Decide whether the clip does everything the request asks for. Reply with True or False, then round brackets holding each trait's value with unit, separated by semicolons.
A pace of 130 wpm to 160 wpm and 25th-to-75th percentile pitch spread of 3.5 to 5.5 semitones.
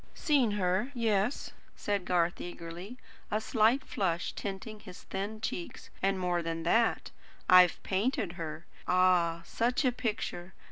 True (135 wpm; 3.9 semitones)